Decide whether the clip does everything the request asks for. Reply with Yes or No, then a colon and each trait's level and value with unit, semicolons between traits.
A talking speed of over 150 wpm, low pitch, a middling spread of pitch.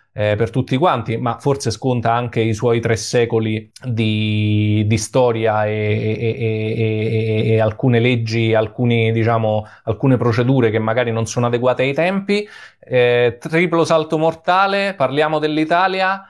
No: average, 145 wpm; low, 115 Hz; average, 3.6 semitones